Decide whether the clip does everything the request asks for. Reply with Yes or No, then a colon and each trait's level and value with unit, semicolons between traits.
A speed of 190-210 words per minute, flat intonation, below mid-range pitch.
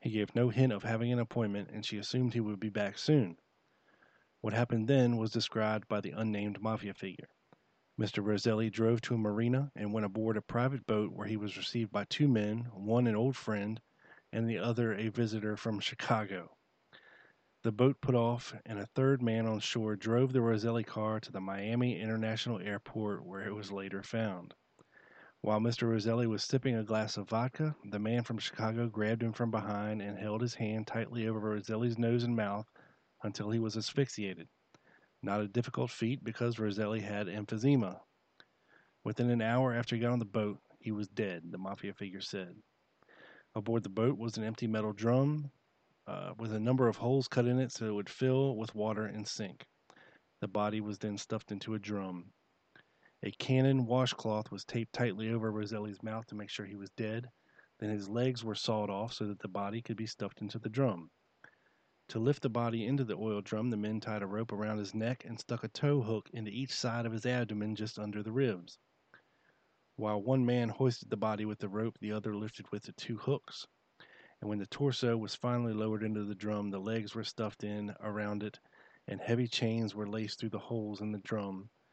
Yes: average, 200 wpm; narrow, 2.1 semitones; low, 110 Hz